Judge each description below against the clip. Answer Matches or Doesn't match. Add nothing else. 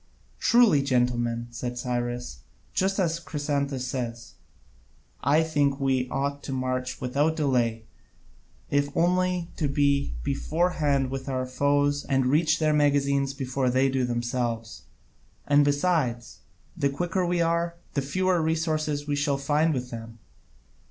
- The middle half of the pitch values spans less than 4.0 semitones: Matches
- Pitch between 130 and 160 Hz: Matches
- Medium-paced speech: Doesn't match